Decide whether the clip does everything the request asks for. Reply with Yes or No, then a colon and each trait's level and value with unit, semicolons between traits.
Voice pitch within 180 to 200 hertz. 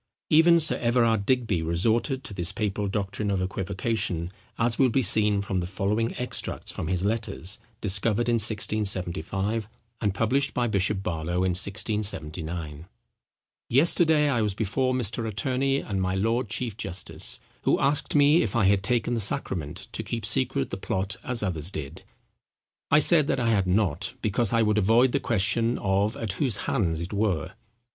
No: low, 105 Hz